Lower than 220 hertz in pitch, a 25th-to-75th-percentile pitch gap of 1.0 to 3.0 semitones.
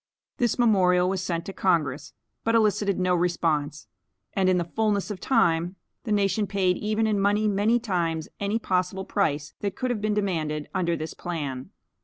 No: high, 190 Hz; average, 3.6 semitones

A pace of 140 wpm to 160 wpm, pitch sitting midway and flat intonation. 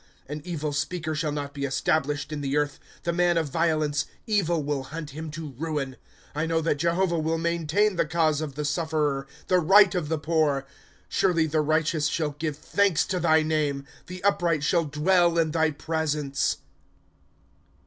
No: average, 185 wpm; medium, 155 Hz; narrow, 2.3 semitones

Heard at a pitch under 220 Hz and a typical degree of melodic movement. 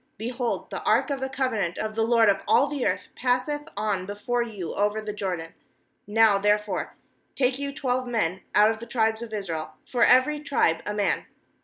No: high, 225 Hz; average, 3.6 semitones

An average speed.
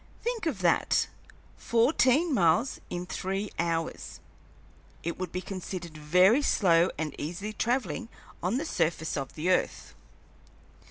No: slow, 125 wpm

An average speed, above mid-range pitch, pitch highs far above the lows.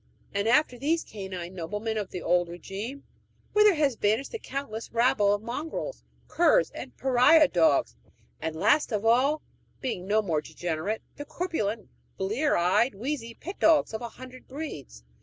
Yes: average, 155 wpm; high, 225 Hz; wide, 6.6 semitones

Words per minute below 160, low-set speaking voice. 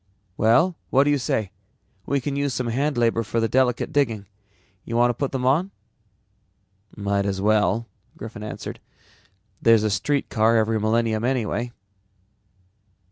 Yes: average, 140 wpm; low, 115 Hz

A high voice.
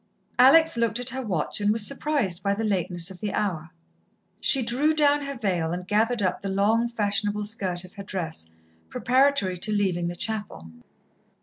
Yes: high, 205 Hz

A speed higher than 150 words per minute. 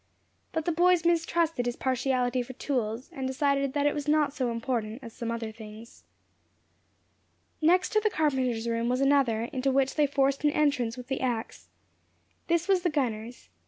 Yes: average, 175 wpm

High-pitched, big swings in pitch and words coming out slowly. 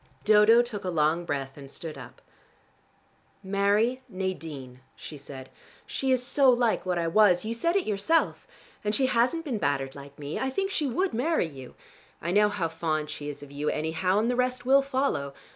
No: high, 195 Hz; wide, 8.6 semitones; average, 195 wpm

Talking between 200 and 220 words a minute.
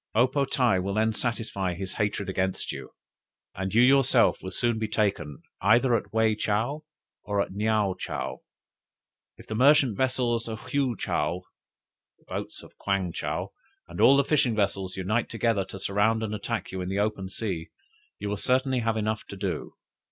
No: average, 180 wpm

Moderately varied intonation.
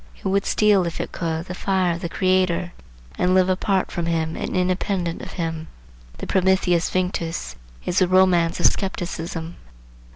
No: narrow, 1.9 semitones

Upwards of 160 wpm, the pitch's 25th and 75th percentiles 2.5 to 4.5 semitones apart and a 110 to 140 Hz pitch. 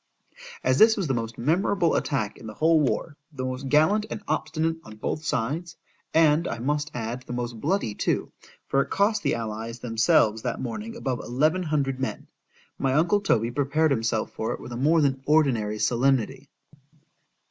No: average, 170 wpm; average, 5.3 semitones; low, 135 Hz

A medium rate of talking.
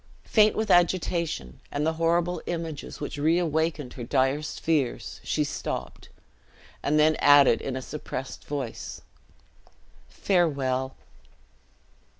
No: slow, 110 wpm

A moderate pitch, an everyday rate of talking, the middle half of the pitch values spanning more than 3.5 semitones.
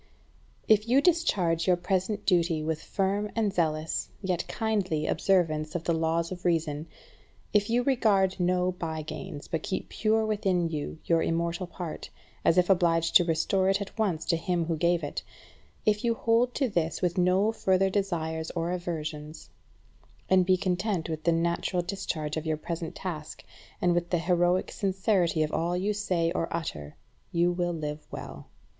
No: medium, 175 Hz; average, 175 wpm; average, 2.9 semitones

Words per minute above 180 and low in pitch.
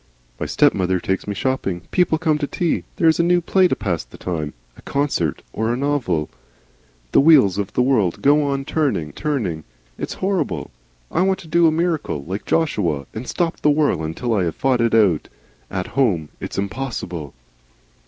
Yes: average, 195 wpm; low, 125 Hz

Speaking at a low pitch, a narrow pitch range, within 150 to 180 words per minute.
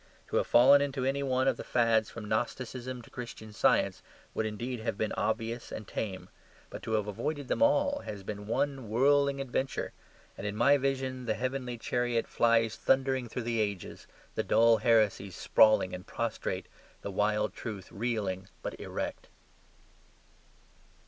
No: low, 115 Hz; average, 3.4 semitones; average, 160 wpm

